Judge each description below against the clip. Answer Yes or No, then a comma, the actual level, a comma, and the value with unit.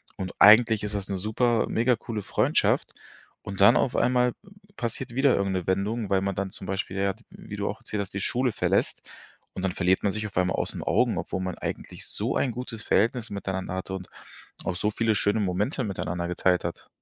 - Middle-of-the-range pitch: No, low, 100 Hz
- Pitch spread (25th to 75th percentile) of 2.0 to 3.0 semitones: No, average, 3.4 semitones